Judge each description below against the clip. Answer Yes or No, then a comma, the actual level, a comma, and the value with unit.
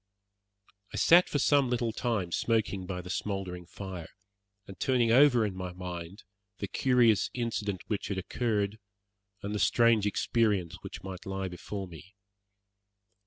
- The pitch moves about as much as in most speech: Yes, average, 4.0 semitones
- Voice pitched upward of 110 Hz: No, low, 100 Hz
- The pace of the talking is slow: No, average, 145 wpm